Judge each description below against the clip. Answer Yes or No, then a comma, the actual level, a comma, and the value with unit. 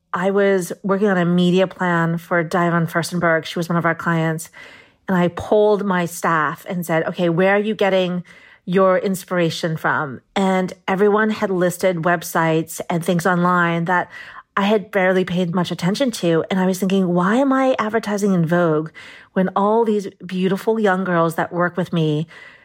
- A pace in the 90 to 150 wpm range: No, average, 175 wpm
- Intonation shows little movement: Yes, narrow, 2.3 semitones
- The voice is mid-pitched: Yes, medium, 180 Hz